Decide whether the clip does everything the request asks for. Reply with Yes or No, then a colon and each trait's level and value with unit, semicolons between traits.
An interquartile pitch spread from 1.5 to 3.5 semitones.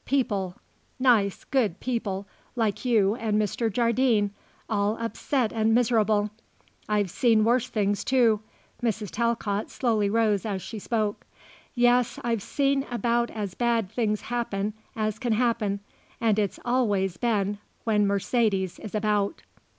Yes: narrow, 2.6 semitones